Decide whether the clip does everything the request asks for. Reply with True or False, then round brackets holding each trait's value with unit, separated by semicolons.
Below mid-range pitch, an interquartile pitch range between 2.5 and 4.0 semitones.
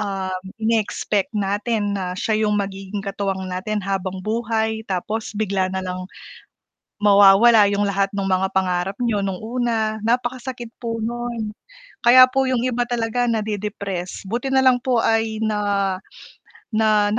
False (210 Hz; 2.9 semitones)